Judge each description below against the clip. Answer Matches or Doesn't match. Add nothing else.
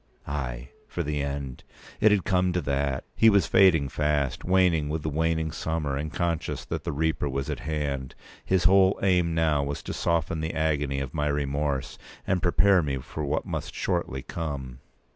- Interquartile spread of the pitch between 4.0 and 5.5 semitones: Doesn't match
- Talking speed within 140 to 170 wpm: Doesn't match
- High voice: Doesn't match